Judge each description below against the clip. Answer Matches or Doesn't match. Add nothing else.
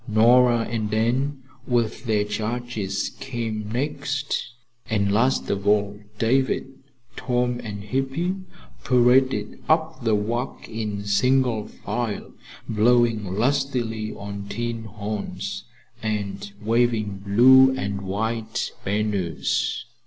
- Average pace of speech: Doesn't match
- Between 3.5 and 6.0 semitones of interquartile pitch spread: Doesn't match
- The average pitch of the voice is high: Doesn't match